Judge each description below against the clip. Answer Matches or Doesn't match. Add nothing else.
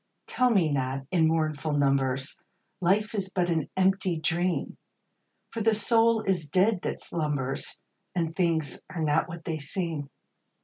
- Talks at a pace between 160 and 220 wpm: Doesn't match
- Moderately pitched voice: Matches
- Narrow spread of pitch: Doesn't match